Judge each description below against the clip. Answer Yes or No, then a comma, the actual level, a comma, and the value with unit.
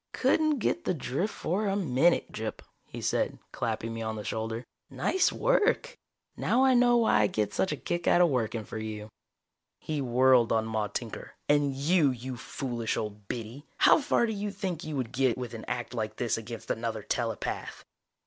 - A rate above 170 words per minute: Yes, average, 190 wpm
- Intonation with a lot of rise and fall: Yes, wide, 8.2 semitones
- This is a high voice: No, low, 125 Hz